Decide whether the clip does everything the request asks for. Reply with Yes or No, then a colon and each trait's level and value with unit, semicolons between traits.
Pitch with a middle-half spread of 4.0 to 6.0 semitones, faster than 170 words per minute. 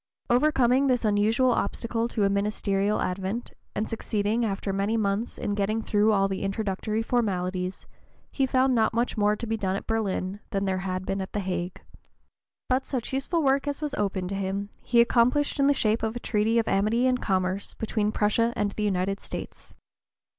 No: average, 3.3 semitones; average, 190 wpm